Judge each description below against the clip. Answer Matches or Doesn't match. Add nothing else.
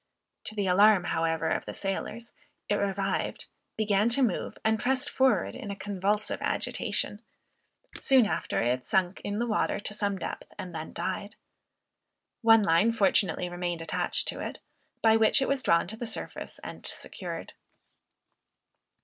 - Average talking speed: Matches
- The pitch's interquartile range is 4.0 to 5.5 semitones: Doesn't match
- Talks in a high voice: Matches